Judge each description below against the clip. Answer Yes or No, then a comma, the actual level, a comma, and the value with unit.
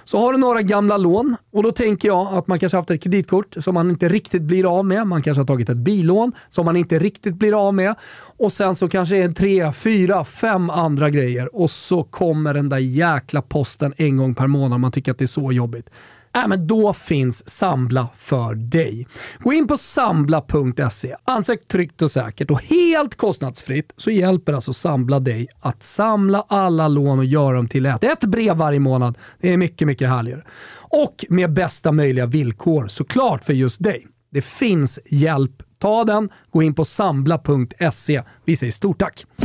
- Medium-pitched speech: Yes, medium, 165 Hz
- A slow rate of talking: No, fast, 195 wpm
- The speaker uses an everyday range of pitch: No, wide, 6.3 semitones